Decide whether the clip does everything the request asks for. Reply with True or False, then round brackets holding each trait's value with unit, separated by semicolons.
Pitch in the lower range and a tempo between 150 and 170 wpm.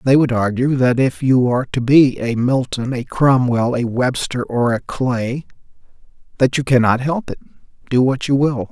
False (125 Hz; 185 wpm)